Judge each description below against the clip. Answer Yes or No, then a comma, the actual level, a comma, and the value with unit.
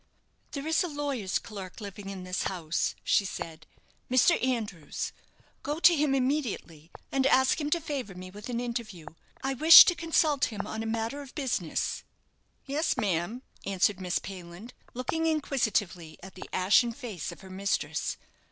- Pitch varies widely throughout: Yes, wide, 6.9 semitones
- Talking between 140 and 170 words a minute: Yes, average, 160 wpm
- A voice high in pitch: Yes, high, 230 Hz